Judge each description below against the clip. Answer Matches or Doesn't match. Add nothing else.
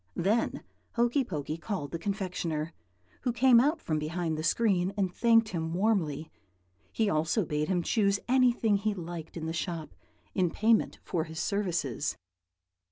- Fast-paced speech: Doesn't match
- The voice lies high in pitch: Doesn't match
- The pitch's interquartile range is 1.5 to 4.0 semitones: Doesn't match